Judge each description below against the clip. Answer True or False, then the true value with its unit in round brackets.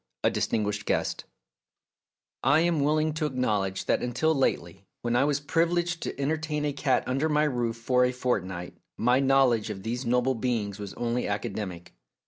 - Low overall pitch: True (125 Hz)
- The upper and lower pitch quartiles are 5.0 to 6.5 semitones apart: True (5.5 semitones)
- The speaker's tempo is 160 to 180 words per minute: True (170 wpm)